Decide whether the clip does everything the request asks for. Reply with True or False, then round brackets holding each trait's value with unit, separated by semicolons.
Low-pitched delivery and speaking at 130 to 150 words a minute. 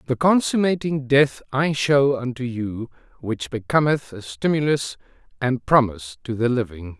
True (125 Hz; 135 wpm)